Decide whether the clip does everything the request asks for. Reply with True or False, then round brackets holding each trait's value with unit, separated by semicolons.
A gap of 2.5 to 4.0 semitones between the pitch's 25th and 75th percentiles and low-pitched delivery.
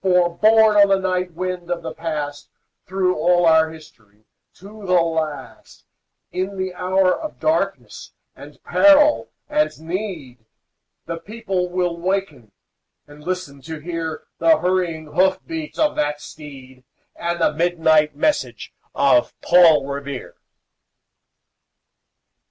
False (3.6 semitones; 175 Hz)